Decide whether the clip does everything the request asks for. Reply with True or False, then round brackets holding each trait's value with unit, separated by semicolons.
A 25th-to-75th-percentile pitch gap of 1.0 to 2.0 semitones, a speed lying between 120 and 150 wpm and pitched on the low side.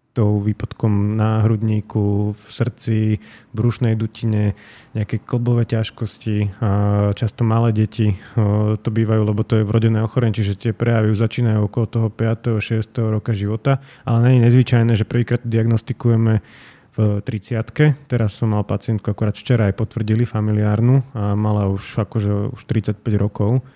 True (1.7 semitones; 145 wpm; 110 Hz)